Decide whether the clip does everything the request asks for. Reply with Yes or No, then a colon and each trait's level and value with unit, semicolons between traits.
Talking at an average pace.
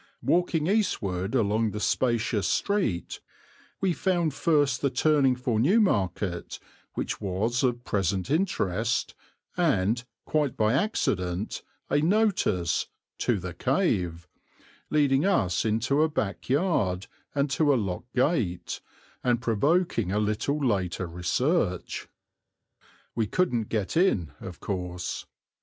No: slow, 115 wpm